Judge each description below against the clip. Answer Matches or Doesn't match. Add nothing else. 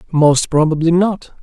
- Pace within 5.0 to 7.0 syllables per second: Doesn't match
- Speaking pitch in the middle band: Matches